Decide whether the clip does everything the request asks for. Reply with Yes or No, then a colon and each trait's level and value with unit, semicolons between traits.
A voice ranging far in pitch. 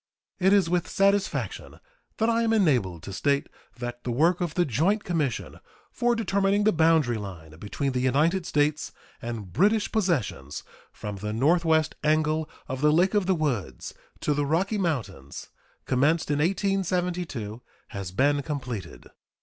Yes: wide, 7.1 semitones